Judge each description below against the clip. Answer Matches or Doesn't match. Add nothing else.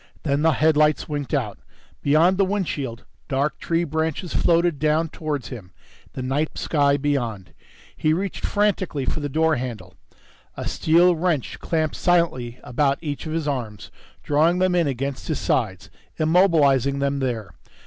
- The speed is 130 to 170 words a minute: Matches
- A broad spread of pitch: Doesn't match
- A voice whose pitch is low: Doesn't match